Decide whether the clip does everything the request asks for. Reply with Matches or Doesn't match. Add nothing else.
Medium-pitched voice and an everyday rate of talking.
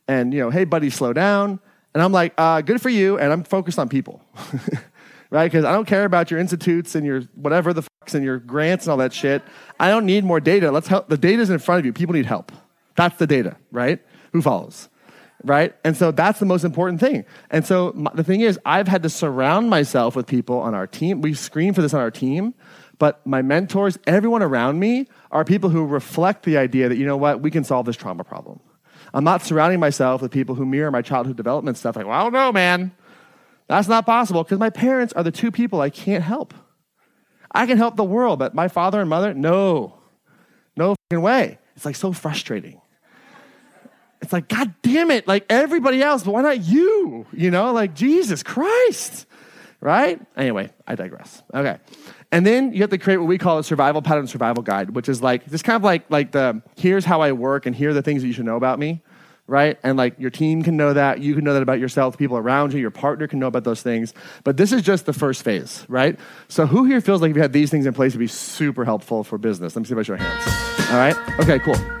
Doesn't match